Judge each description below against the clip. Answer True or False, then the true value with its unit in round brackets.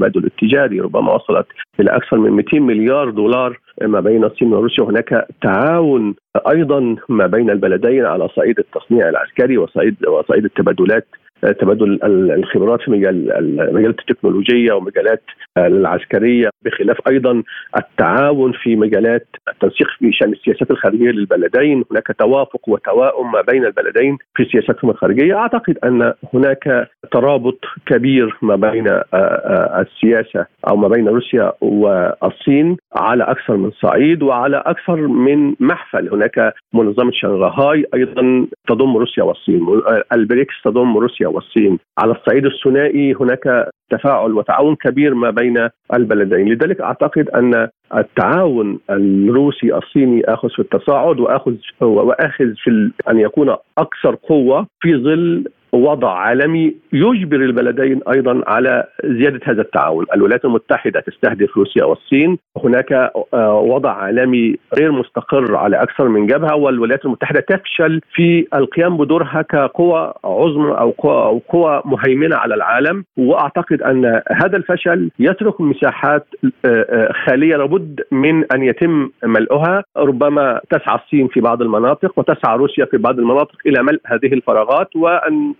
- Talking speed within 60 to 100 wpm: False (125 wpm)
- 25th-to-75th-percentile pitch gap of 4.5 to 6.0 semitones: True (5.1 semitones)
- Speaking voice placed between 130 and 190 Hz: True (135 Hz)